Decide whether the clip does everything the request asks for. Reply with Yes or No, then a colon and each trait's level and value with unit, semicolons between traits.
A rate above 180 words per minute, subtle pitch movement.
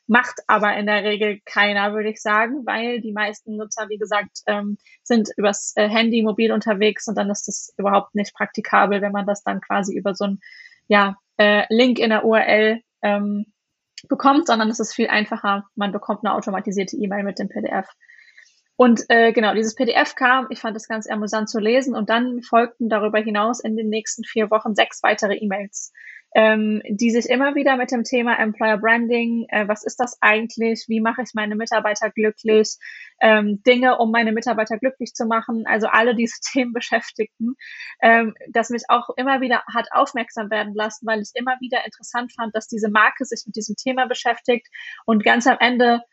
Yes: fast, 190 wpm; narrow, 2.1 semitones